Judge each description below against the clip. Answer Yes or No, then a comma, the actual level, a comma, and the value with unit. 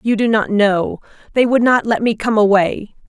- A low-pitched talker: No, high, 215 Hz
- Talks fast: Yes, fast, 215 wpm